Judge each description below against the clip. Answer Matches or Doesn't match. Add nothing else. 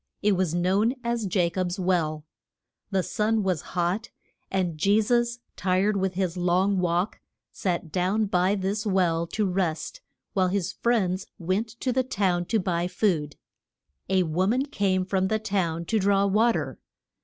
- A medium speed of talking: Matches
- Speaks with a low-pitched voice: Doesn't match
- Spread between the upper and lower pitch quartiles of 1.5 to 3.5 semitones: Matches